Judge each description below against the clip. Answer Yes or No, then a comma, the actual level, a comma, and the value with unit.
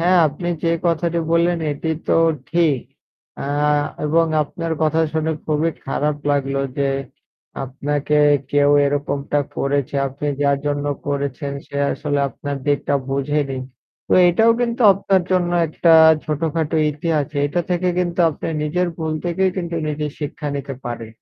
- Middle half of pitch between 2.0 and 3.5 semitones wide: Yes, average, 2.9 semitones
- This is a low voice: No, medium, 150 Hz